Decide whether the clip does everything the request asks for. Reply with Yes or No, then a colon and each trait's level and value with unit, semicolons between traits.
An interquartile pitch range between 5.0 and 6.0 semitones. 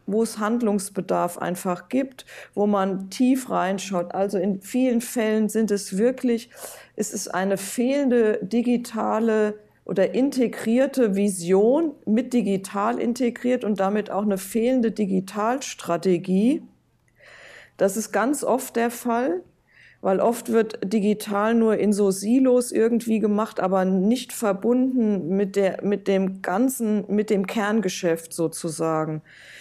No: average, 3.5 semitones